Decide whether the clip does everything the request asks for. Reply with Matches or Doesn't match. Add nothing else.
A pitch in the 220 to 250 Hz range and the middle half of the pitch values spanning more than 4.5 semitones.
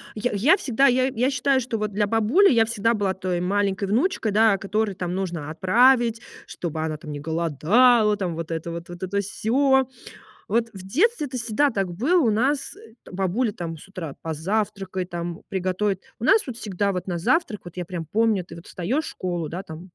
Doesn't match